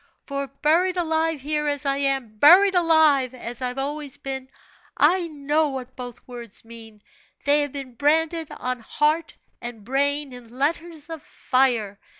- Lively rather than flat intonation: No, average, 3.7 semitones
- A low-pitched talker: No, very high, 280 Hz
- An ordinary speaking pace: Yes, average, 155 wpm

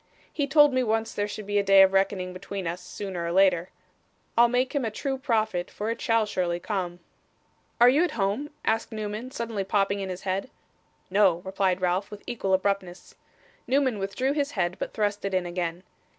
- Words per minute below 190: No, average, 195 wpm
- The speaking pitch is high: Yes, high, 200 Hz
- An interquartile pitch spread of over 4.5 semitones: No, average, 3.6 semitones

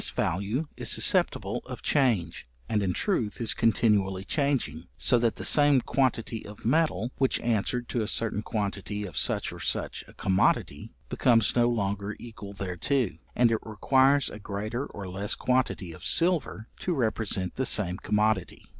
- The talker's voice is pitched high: No, low, 110 Hz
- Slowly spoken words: No, average, 165 wpm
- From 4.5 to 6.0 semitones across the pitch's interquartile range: No, average, 4.1 semitones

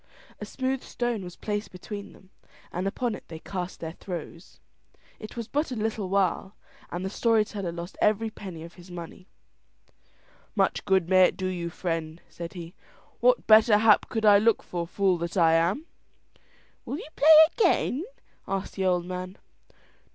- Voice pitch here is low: No, high, 190 Hz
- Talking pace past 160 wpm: Yes, average, 175 wpm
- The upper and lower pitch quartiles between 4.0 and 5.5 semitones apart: No, average, 3.6 semitones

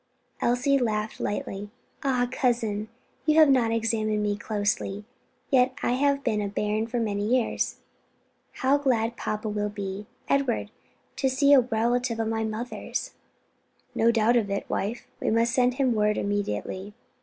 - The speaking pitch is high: Yes, high, 225 Hz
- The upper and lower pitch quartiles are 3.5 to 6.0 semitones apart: No, average, 3.0 semitones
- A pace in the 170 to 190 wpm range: No, average, 160 wpm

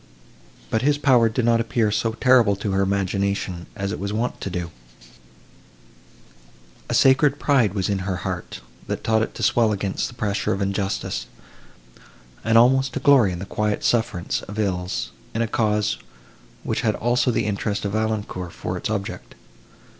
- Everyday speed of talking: Yes, average, 170 wpm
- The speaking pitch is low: Yes, low, 105 Hz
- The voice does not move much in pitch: No, average, 3.1 semitones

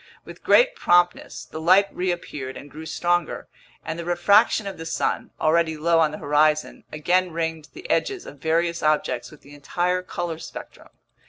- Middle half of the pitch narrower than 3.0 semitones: Yes, narrow, 2.5 semitones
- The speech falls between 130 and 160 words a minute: No, average, 170 wpm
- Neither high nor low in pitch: Yes, medium, 165 Hz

